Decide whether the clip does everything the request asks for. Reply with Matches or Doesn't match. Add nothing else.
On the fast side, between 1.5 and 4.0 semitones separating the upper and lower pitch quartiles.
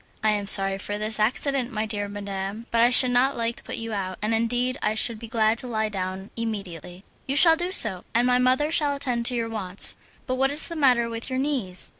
Matches